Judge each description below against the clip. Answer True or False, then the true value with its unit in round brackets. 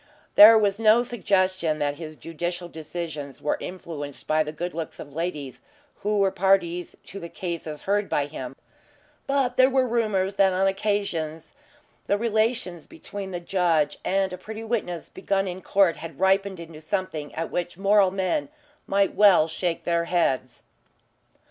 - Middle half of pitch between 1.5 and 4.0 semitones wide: True (3.6 semitones)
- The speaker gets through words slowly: False (160 wpm)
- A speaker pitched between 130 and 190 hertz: True (185 Hz)